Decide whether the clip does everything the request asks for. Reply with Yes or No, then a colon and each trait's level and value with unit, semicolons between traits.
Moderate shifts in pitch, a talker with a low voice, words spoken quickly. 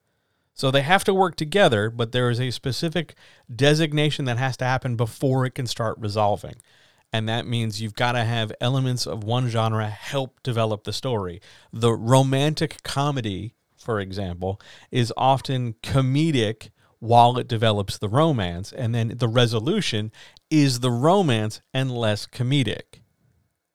No: average, 3.4 semitones; low, 120 Hz; average, 150 wpm